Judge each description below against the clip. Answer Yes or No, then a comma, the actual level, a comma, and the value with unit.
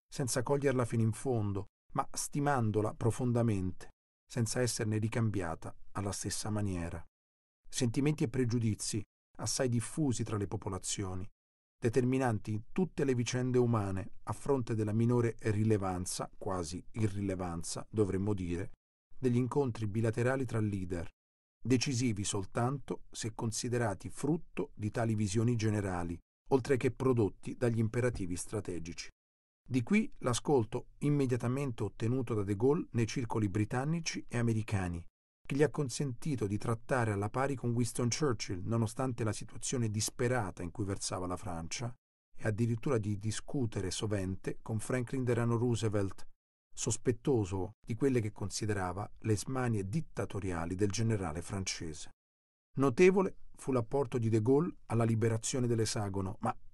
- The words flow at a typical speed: Yes, average, 125 wpm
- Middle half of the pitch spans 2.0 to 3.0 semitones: No, average, 4.0 semitones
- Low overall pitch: Yes, low, 115 Hz